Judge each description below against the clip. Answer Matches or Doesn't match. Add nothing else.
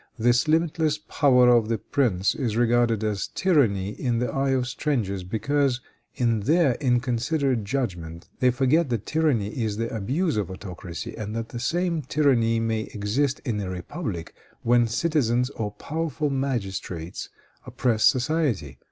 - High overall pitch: Doesn't match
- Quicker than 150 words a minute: Doesn't match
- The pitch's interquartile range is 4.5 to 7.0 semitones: Matches